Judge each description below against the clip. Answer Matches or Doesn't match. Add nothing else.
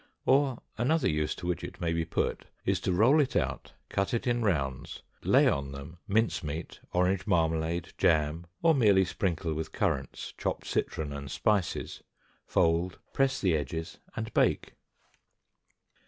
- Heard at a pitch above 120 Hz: Doesn't match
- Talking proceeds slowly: Doesn't match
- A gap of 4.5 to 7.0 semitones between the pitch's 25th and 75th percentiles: Matches